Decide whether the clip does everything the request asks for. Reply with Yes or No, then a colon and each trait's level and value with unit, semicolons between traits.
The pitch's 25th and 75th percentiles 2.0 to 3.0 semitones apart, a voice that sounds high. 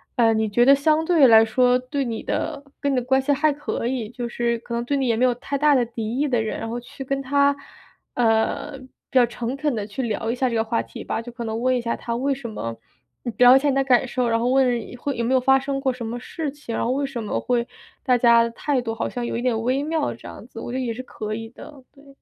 Yes: average, 2.7 semitones; very high, 250 Hz